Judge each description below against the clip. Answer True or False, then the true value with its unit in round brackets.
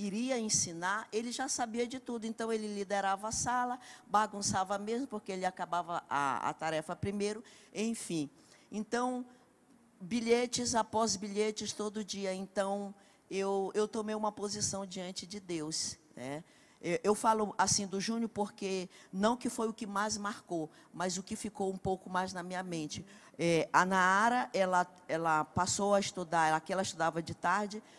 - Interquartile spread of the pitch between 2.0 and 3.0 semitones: False (3.4 semitones)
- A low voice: False (205 Hz)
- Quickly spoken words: False (160 wpm)